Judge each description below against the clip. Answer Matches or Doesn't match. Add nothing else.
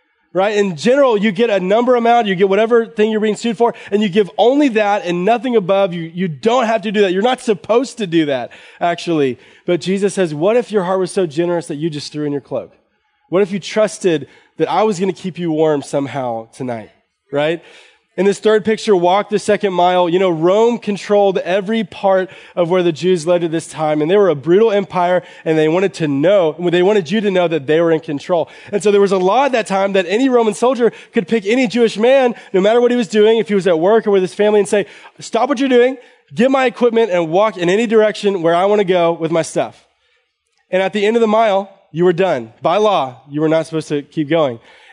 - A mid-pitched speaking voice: Doesn't match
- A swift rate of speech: Matches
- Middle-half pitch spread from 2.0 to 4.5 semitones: Matches